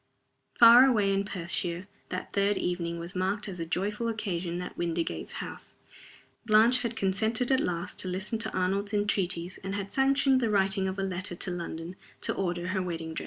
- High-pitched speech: Yes, high, 195 Hz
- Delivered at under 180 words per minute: No, average, 185 wpm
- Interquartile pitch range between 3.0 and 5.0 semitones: Yes, average, 3.3 semitones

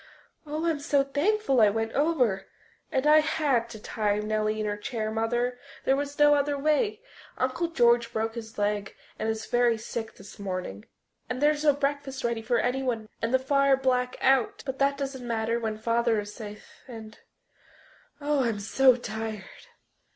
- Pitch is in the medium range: No, high, 240 Hz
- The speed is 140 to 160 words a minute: No, average, 175 wpm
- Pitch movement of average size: Yes, average, 4.0 semitones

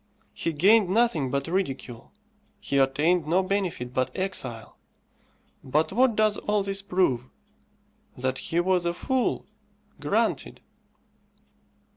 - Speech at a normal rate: No, slow, 115 wpm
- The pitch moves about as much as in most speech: No, wide, 6.5 semitones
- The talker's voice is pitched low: No, medium, 175 Hz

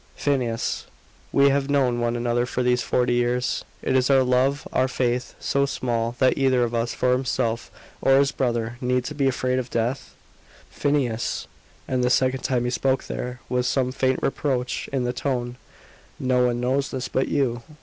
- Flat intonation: Yes, narrow, 1.6 semitones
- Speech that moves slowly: No, average, 175 wpm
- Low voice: Yes, low, 125 Hz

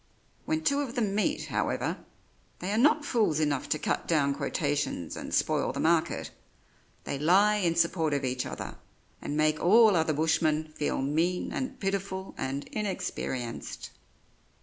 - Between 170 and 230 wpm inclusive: No, average, 150 wpm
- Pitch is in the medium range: Yes, medium, 170 Hz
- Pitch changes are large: Yes, wide, 6.0 semitones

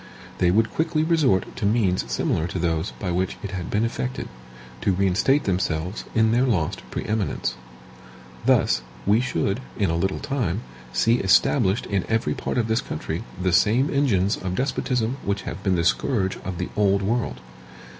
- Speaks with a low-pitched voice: Yes, low, 100 Hz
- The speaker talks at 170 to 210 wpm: Yes, average, 175 wpm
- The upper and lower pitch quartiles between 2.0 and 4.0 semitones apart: No, average, 4.5 semitones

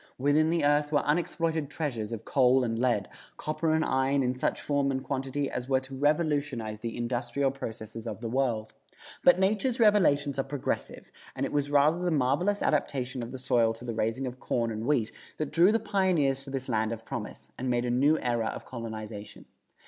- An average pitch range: Yes, average, 3.8 semitones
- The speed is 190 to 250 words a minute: Yes, average, 200 wpm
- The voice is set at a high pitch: No, low, 135 Hz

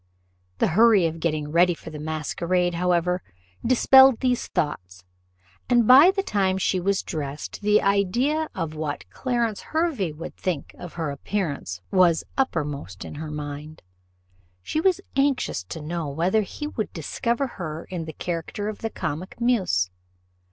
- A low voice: No, medium, 180 Hz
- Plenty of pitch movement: Yes, wide, 6.7 semitones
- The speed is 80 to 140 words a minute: No, average, 150 wpm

